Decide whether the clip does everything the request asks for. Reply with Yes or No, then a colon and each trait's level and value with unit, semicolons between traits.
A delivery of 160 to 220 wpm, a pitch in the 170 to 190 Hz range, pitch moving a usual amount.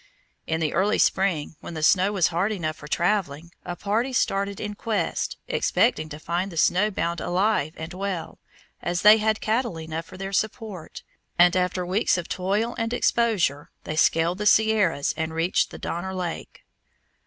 Yes: average, 175 wpm; medium, 185 Hz; average, 4.2 semitones